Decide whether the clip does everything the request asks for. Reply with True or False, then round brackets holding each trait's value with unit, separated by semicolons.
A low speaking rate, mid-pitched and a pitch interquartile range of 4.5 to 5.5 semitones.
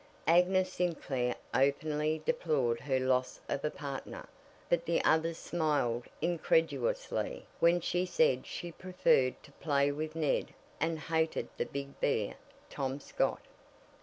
False (130 wpm; 155 Hz; 3.8 semitones)